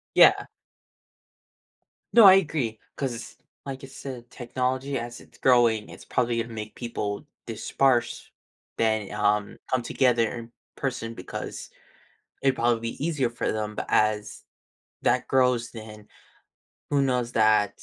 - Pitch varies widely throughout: No, average, 3.1 semitones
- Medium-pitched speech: No, low, 120 Hz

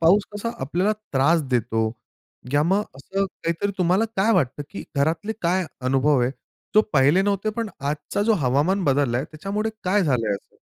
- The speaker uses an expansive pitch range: Yes, wide, 6.2 semitones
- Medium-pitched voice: Yes, medium, 170 Hz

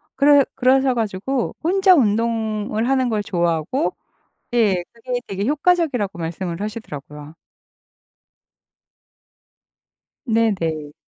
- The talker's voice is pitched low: No, high, 225 Hz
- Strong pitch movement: Yes, wide, 5.9 semitones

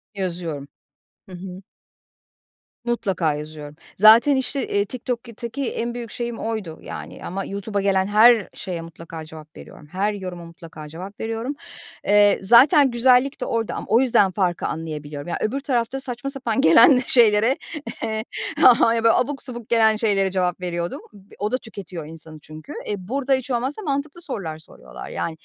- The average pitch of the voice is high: Yes, high, 210 Hz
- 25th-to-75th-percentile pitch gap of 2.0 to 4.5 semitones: No, wide, 5.6 semitones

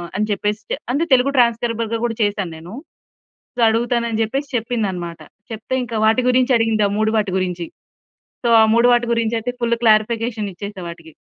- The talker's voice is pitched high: Yes, high, 225 Hz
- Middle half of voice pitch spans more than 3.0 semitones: No, narrow, 2.4 semitones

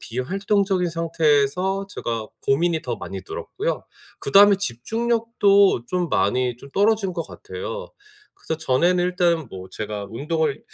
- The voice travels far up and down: Yes, wide, 7.3 semitones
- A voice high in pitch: No, medium, 170 Hz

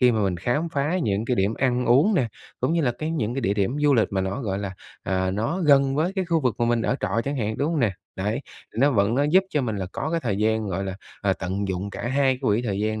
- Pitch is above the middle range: No, low, 115 Hz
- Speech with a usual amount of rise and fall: No, wide, 5.9 semitones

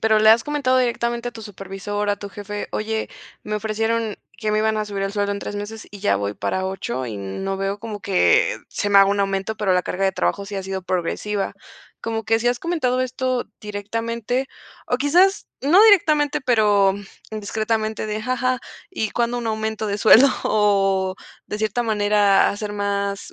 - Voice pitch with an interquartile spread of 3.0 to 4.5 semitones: No, narrow, 2.6 semitones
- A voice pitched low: No, high, 215 Hz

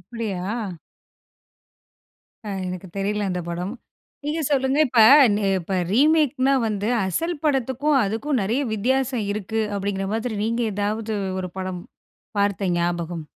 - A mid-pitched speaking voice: No, high, 215 Hz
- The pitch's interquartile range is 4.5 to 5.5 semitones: Yes, average, 5.2 semitones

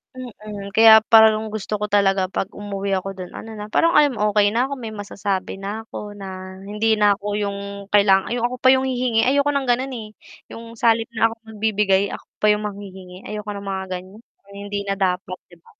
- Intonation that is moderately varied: No, narrow, 2.2 semitones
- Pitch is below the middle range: No, high, 210 Hz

